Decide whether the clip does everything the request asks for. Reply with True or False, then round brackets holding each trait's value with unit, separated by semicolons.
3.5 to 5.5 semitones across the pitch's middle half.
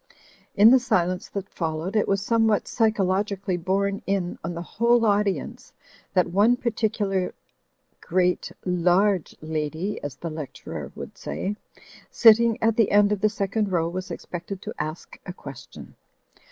False (3.1 semitones)